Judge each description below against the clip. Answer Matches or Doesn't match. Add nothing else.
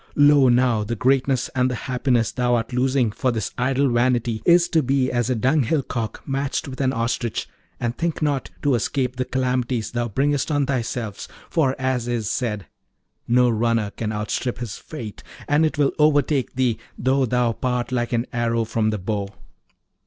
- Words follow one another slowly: Doesn't match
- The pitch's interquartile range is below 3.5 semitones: Matches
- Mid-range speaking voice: Doesn't match